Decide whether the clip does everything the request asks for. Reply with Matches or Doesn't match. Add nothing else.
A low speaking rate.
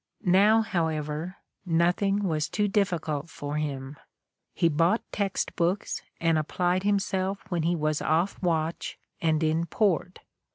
Matches